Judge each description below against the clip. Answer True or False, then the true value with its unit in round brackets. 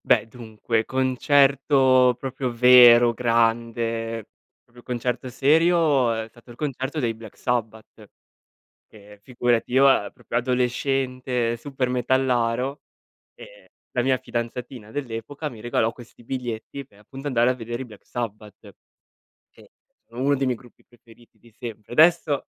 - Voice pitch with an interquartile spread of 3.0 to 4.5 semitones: False (2.4 semitones)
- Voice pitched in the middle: False (125 Hz)